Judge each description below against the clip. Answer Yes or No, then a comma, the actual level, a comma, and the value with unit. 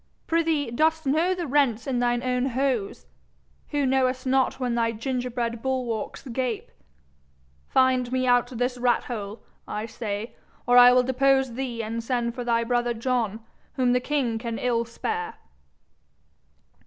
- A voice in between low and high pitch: No, very high, 250 Hz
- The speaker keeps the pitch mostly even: Yes, narrow, 2.2 semitones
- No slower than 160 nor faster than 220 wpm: No, average, 150 wpm